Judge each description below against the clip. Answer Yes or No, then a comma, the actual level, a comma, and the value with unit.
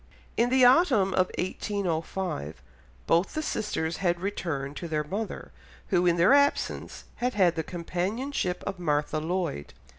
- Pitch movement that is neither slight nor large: Yes, average, 4.3 semitones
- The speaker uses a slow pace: No, average, 145 wpm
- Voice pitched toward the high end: No, medium, 180 Hz